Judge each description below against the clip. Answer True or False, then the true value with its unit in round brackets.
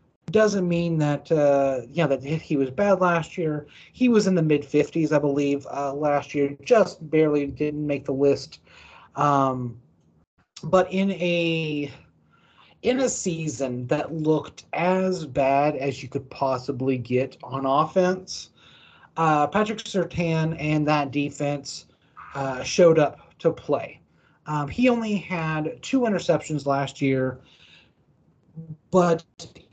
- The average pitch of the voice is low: False (150 Hz)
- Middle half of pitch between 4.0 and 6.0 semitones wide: False (3.5 semitones)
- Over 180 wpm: False (135 wpm)